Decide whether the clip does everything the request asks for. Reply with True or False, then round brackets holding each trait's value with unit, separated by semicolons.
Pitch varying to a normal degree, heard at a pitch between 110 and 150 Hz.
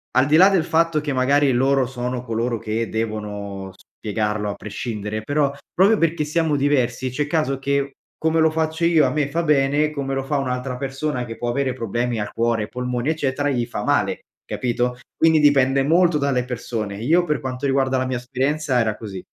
True (3.8 semitones; 135 Hz)